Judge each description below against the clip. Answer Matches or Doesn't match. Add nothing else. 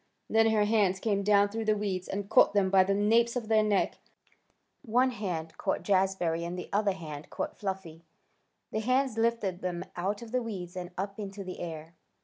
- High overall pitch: Matches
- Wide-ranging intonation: Doesn't match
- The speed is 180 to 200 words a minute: Matches